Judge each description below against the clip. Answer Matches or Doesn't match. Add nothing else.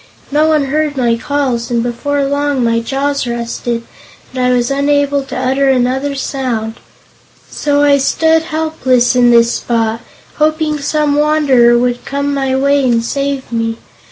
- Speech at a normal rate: Matches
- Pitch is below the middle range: Doesn't match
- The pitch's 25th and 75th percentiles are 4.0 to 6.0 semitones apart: Doesn't match